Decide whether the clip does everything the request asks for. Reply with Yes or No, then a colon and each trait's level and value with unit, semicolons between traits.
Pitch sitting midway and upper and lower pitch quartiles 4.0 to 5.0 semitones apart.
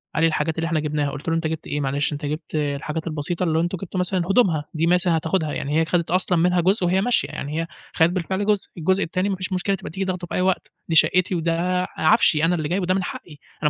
No: medium, 170 Hz; average, 2.7 semitones